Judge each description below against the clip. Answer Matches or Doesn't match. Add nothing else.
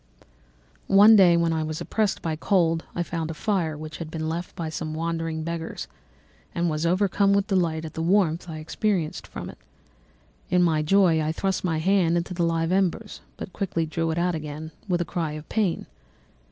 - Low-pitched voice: Doesn't match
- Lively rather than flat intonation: Doesn't match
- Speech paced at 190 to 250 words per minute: Matches